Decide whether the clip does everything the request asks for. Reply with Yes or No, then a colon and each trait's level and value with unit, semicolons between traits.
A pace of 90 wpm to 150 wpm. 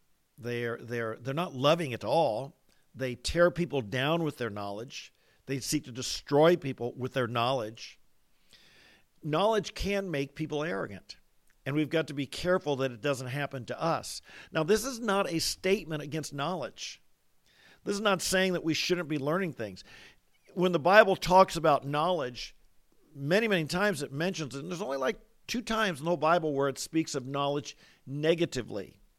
No: average, 175 wpm